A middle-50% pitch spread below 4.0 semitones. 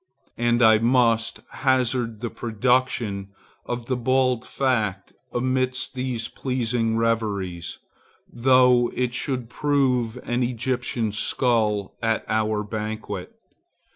Yes: narrow, 2.5 semitones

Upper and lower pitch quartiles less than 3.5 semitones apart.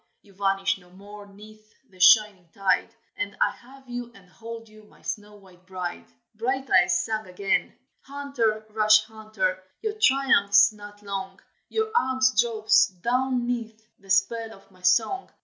Yes: average, 3.1 semitones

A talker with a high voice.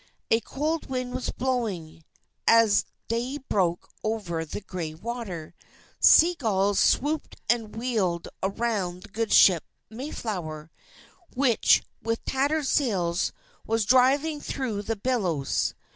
Yes: high, 225 Hz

